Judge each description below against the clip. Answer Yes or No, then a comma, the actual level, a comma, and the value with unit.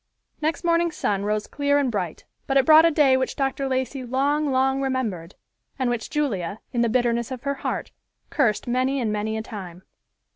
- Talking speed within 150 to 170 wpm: No, average, 190 wpm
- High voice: Yes, very high, 260 Hz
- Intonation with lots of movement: No, average, 4.2 semitones